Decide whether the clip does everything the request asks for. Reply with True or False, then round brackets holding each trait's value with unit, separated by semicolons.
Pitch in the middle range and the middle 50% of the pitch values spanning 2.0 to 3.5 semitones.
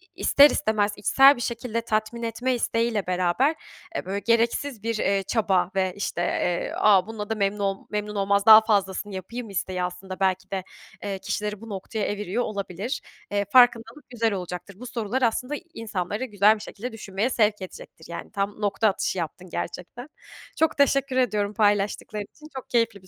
False (210 Hz; 3.0 semitones)